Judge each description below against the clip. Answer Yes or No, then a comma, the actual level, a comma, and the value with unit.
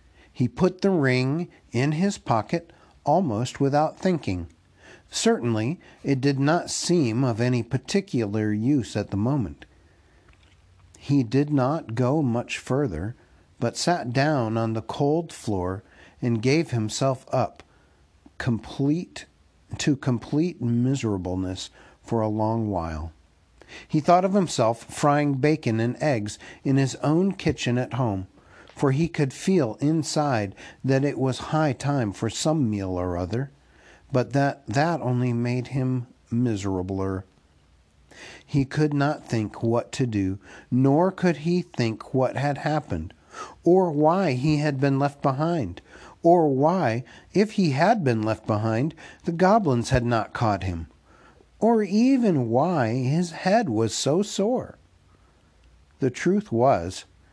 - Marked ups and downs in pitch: Yes, wide, 6.3 semitones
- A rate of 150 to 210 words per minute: No, slow, 135 wpm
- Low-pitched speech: Yes, low, 130 Hz